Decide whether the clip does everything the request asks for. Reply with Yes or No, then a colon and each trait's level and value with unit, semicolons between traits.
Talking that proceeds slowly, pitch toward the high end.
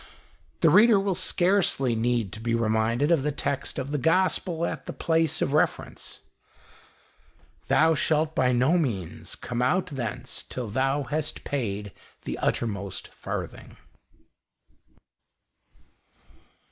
No: slow, 130 wpm; low, 135 Hz